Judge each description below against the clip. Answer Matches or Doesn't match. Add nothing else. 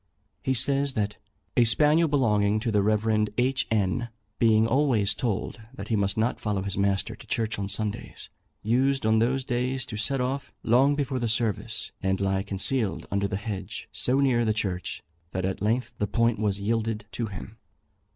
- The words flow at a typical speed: Matches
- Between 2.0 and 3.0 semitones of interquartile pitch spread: Doesn't match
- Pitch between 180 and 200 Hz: Doesn't match